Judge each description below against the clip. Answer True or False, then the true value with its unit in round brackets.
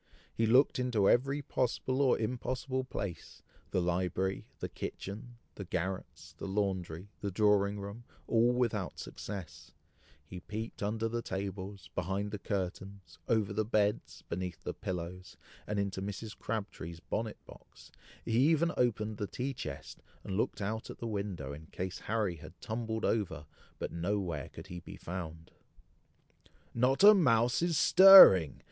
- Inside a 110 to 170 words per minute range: True (150 wpm)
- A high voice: False (100 Hz)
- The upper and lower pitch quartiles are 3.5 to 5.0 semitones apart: True (3.8 semitones)